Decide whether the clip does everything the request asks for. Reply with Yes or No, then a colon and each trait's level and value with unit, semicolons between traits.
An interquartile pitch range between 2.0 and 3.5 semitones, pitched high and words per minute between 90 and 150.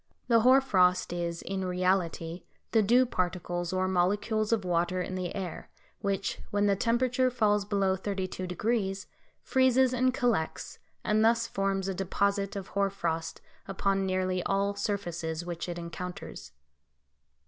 Yes: average, 2.8 semitones; high, 195 Hz; average, 140 wpm